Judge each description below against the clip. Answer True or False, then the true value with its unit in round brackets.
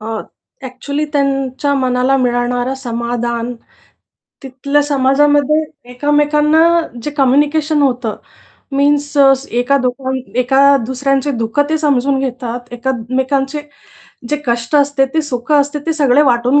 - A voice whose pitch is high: True (270 Hz)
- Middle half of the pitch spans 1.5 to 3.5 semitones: True (2.8 semitones)